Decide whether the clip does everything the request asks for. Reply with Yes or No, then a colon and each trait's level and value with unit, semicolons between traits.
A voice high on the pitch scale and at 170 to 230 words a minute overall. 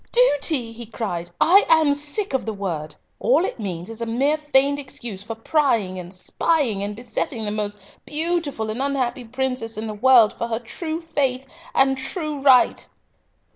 Yes: very high, 250 Hz; average, 175 wpm